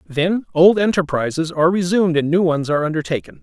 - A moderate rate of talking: Yes, average, 175 wpm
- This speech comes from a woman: No, male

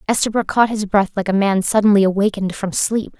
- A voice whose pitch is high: Yes, high, 205 Hz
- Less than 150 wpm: No, fast, 205 wpm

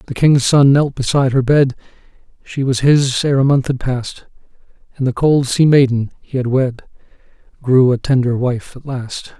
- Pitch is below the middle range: Yes, low, 130 Hz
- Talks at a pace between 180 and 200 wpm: Yes, average, 185 wpm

